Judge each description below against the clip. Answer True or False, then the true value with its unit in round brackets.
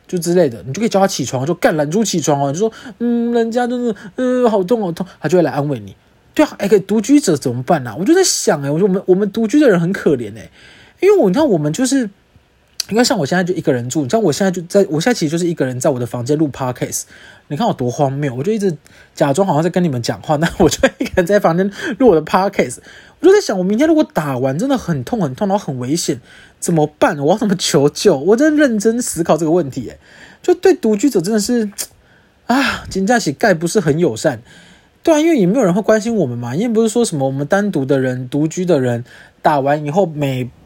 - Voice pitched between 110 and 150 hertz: False (185 Hz)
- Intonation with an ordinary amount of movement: False (7.3 semitones)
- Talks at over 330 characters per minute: True (380 characters per minute)